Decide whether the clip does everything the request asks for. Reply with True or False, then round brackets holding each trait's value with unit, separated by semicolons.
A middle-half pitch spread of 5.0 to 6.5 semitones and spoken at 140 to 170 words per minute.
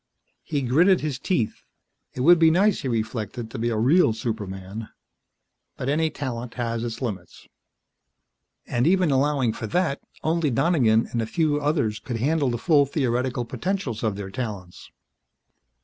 True (5.4 semitones; 160 wpm)